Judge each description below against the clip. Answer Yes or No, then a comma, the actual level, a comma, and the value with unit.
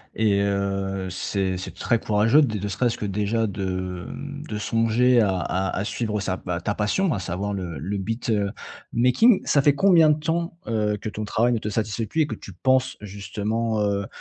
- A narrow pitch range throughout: No, average, 3.3 semitones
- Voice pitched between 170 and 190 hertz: No, low, 105 Hz